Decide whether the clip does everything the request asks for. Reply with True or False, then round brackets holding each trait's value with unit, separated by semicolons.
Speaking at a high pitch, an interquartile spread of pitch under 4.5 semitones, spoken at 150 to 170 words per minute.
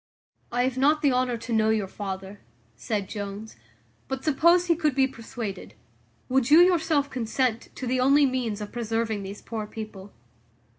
True (240 Hz; 4.1 semitones; 165 wpm)